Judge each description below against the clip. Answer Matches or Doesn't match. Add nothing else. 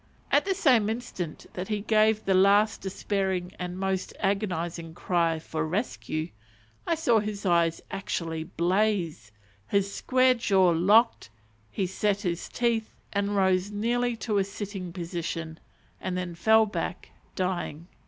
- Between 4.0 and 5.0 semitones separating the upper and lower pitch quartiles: Doesn't match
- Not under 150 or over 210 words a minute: Doesn't match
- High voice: Matches